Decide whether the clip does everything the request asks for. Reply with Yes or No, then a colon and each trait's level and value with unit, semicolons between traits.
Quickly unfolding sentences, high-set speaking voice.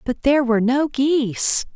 No: average, 170 wpm; very high, 260 Hz